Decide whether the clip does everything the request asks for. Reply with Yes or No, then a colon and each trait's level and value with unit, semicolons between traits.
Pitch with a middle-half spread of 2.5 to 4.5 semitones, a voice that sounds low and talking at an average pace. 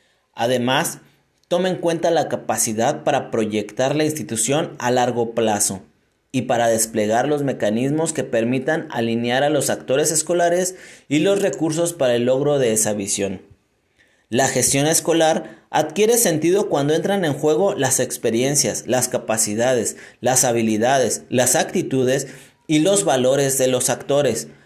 No: average, 5.0 semitones; low, 130 Hz; average, 140 wpm